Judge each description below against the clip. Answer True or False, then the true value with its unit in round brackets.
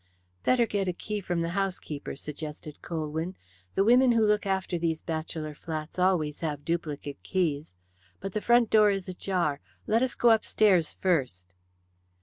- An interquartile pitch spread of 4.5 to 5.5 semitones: True (4.8 semitones)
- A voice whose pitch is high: False (175 Hz)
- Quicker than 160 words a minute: False (155 wpm)